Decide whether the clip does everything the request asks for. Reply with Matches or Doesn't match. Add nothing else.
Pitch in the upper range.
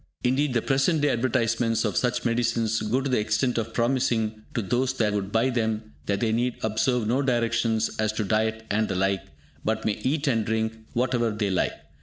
Doesn't match